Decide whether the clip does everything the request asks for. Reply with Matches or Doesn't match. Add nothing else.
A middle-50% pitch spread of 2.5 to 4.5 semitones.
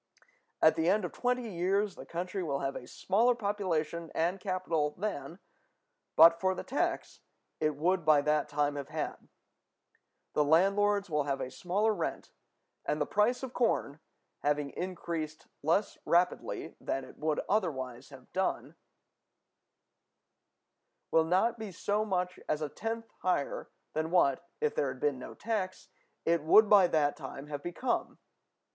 Doesn't match